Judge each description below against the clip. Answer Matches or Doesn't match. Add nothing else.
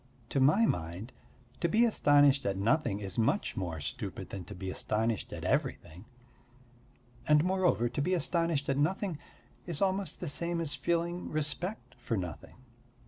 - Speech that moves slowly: Doesn't match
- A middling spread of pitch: Doesn't match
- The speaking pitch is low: Doesn't match